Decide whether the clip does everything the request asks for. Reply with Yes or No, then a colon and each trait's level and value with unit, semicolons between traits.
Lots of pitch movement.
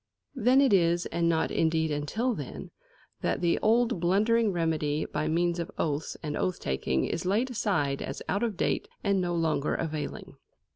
No: average, 5.0 semitones